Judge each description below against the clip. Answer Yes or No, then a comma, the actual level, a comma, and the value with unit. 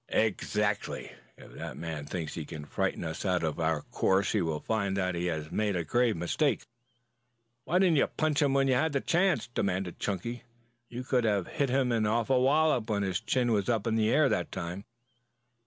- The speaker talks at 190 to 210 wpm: Yes, average, 200 wpm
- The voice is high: No, low, 105 Hz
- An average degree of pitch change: No, wide, 6.3 semitones